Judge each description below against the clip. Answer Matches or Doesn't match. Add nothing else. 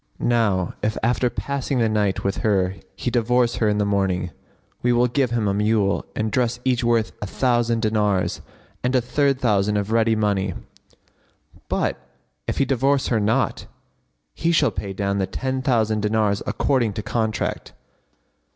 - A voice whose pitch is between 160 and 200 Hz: Doesn't match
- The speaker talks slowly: Doesn't match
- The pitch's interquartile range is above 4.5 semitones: Doesn't match